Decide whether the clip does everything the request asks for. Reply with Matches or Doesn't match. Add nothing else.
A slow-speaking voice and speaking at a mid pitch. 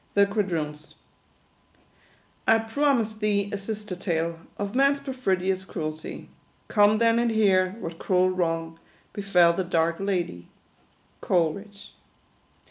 Doesn't match